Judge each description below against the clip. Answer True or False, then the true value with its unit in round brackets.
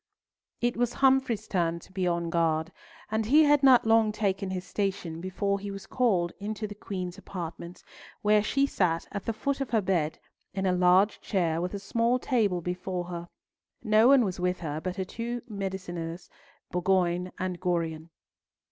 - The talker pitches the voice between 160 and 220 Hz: True (190 Hz)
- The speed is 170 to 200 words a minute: True (175 wpm)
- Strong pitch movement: False (3.7 semitones)